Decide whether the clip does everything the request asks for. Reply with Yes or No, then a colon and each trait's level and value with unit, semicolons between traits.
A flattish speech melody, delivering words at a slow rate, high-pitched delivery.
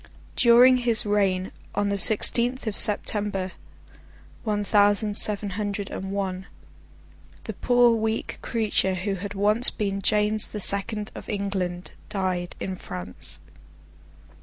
Yes: narrow, 2.0 semitones; slow, 125 wpm; high, 205 Hz